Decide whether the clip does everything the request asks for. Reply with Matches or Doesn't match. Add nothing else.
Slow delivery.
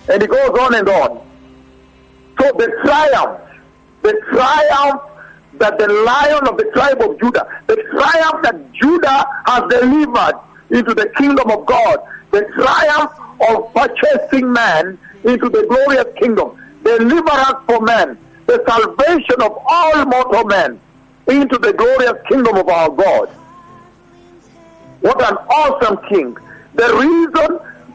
Matches